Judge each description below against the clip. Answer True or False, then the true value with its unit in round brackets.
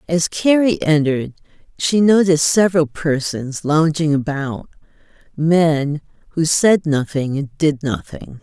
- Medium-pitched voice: True (155 Hz)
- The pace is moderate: False (105 wpm)